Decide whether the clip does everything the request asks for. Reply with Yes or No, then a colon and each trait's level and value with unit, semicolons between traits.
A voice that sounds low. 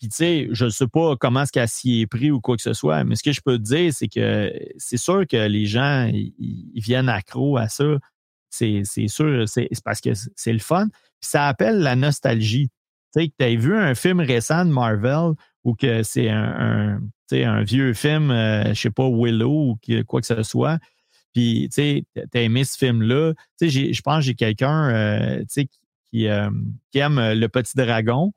Yes: low, 125 Hz